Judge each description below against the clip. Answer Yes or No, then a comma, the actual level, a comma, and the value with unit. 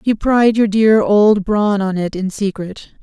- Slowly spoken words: No, average, 200 wpm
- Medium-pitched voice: No, high, 205 Hz